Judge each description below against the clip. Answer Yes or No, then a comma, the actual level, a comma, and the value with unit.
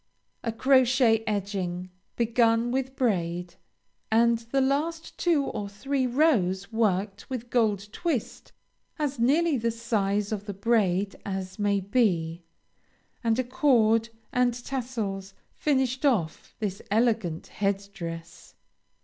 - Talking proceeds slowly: Yes, slow, 120 wpm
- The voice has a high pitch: Yes, high, 225 Hz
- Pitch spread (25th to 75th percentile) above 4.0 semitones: Yes, average, 4.4 semitones